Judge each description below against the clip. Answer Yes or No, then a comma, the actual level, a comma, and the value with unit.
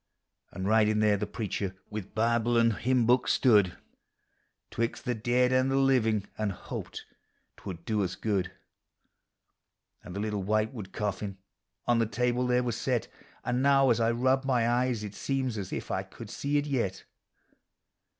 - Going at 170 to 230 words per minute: Yes, average, 180 wpm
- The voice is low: Yes, low, 115 Hz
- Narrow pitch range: No, average, 3.2 semitones